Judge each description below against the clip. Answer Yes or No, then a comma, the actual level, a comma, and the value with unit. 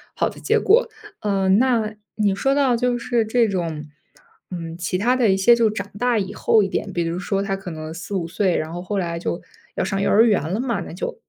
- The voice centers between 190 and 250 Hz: Yes, high, 195 Hz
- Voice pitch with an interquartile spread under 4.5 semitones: No, average, 4.8 semitones